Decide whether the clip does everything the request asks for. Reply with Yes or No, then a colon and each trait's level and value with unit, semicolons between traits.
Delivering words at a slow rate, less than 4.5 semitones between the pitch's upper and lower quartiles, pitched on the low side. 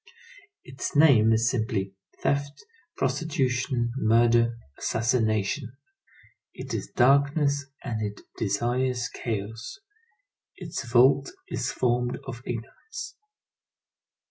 Yes: slow, 90 wpm; average, 3.5 semitones; low, 120 Hz